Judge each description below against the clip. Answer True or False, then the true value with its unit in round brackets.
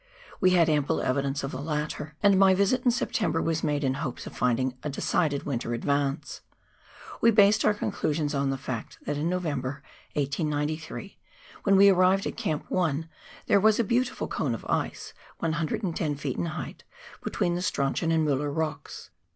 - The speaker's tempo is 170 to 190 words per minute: True (175 wpm)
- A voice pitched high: False (155 Hz)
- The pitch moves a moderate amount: True (4.6 semitones)